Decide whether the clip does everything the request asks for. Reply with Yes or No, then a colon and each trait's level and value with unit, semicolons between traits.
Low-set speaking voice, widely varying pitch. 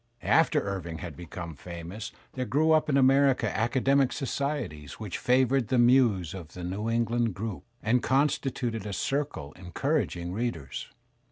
Yes: low, 115 Hz; wide, 6.9 semitones